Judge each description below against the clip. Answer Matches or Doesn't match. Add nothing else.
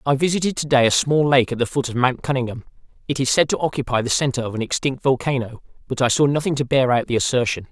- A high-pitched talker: Doesn't match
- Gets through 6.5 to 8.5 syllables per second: Matches